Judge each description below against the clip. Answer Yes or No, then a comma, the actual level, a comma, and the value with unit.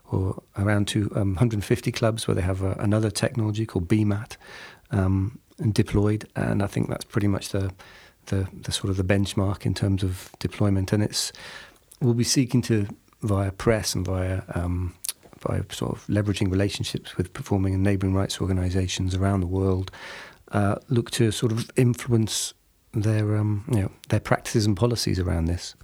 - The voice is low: Yes, low, 100 Hz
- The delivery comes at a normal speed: Yes, average, 175 wpm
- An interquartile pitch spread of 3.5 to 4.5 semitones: No, average, 2.9 semitones